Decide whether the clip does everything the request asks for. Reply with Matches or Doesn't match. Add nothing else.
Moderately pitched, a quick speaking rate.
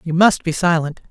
Matches